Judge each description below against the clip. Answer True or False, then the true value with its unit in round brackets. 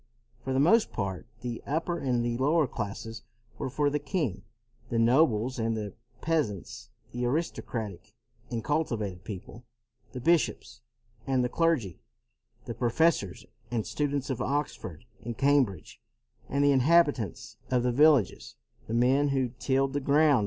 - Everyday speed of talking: True (145 wpm)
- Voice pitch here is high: False (130 Hz)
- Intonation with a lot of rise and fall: False (4.2 semitones)